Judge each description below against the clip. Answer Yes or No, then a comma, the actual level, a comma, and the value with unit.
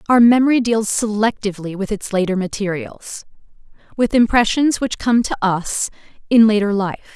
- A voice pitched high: Yes, high, 215 Hz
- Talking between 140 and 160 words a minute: Yes, average, 145 wpm